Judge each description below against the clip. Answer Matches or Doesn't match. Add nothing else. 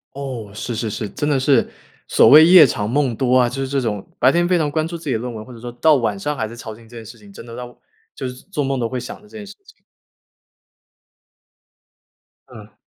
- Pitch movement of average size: Matches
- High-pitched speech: Doesn't match